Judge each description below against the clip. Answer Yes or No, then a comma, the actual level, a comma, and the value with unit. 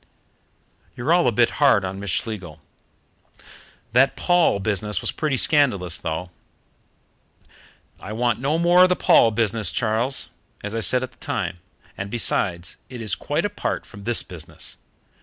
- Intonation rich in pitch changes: Yes, wide, 5.7 semitones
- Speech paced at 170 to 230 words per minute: No, average, 155 wpm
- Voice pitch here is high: No, low, 115 Hz